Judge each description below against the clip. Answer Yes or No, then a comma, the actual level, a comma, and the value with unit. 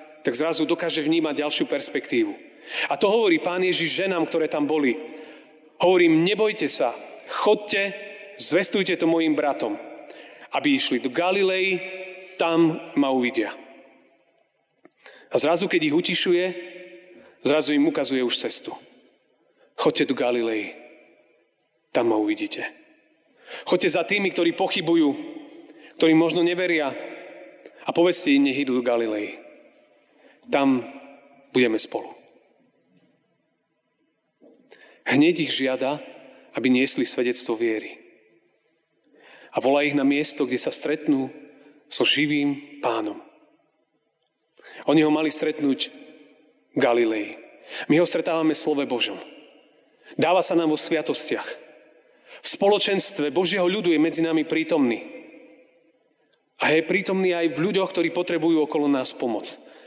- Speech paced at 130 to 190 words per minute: No, average, 115 wpm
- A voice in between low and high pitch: Yes, medium, 160 Hz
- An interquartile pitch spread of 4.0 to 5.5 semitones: Yes, average, 4.3 semitones